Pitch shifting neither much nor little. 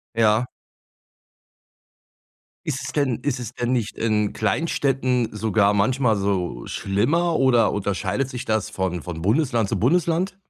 Yes: average, 4.5 semitones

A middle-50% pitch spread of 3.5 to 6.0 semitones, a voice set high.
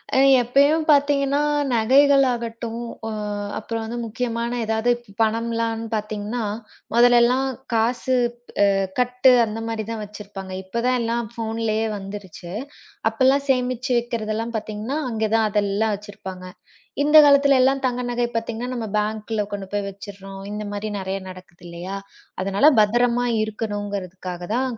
No: average, 3.0 semitones; high, 225 Hz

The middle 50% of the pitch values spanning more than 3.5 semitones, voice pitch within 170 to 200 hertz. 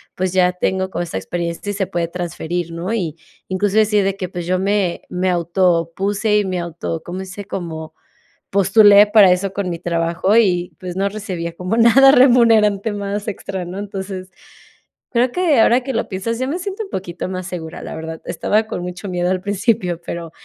No: average, 3.0 semitones; high, 190 Hz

